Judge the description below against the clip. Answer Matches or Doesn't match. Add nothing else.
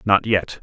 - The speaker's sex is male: Matches